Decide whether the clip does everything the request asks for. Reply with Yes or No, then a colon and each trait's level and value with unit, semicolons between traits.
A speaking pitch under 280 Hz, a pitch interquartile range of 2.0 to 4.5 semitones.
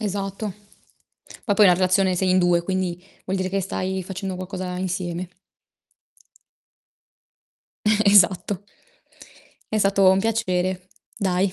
No: medium, 185 Hz; narrow, 1.4 semitones